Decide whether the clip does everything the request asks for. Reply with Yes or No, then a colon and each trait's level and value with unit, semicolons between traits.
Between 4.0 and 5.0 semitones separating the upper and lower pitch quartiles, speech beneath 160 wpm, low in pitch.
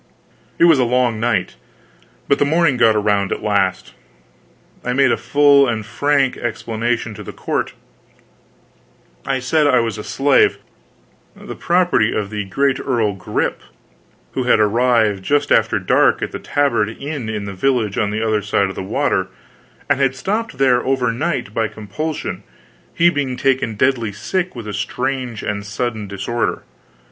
No: average, 4.5 semitones; average, 165 wpm; low, 120 Hz